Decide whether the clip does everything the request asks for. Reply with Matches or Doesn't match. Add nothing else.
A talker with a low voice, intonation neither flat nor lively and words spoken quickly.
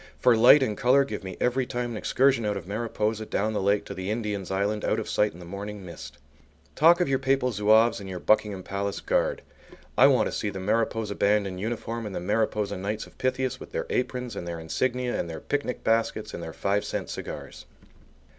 Matches